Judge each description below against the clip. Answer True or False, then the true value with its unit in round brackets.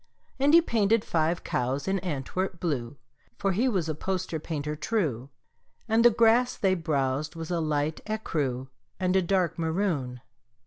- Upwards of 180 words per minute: False (160 wpm)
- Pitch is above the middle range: False (170 Hz)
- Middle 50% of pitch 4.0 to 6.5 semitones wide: True (5.0 semitones)